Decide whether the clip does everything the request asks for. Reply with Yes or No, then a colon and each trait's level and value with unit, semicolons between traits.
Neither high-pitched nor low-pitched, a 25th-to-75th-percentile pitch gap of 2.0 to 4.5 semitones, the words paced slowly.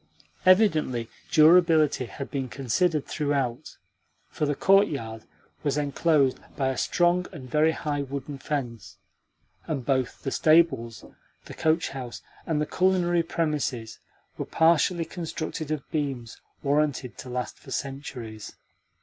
Yes: medium, 145 Hz; average, 3.7 semitones; slow, 125 wpm